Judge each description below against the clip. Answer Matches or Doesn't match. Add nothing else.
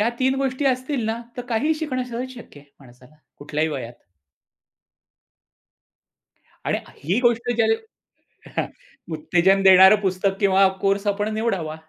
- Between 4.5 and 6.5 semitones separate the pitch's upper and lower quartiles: Matches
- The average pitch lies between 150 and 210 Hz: Matches